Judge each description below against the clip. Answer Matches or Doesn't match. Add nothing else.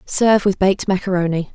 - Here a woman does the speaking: Matches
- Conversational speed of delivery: Matches